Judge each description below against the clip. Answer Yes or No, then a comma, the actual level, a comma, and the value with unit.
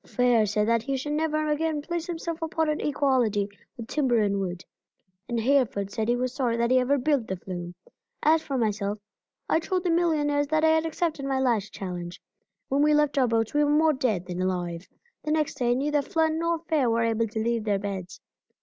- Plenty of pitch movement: Yes, wide, 5.9 semitones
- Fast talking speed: Yes, fast, 215 wpm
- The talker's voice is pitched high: Yes, very high, 260 Hz